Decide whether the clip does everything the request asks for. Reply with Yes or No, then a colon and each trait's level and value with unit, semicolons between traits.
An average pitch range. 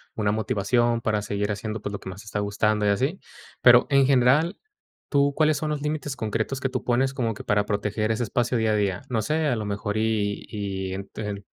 Yes: average, 4.1 semitones